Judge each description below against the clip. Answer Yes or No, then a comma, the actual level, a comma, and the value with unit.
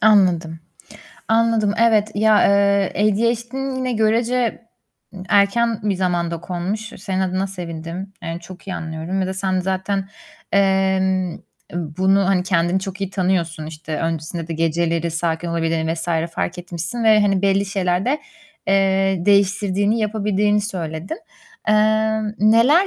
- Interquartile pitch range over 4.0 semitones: No, average, 3.5 semitones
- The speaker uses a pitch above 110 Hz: Yes, high, 190 Hz